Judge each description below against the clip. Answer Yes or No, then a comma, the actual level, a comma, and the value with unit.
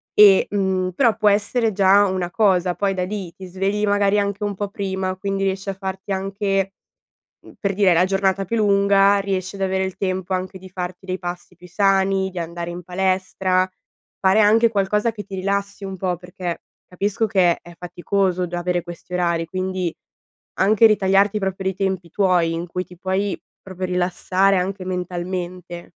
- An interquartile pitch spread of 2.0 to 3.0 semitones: No, narrow, 1.6 semitones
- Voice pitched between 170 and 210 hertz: Yes, high, 190 Hz